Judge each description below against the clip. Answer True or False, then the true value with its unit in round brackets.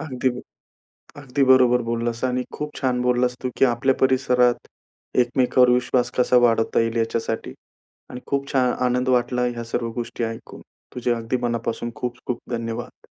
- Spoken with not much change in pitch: True (1.3 semitones)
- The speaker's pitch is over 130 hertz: False (125 Hz)